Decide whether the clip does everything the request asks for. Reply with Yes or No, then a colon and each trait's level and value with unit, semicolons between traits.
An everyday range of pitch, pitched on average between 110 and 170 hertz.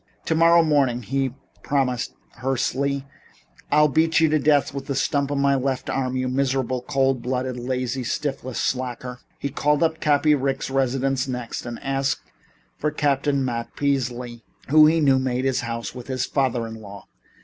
No: narrow, 2.1 semitones; low, 135 Hz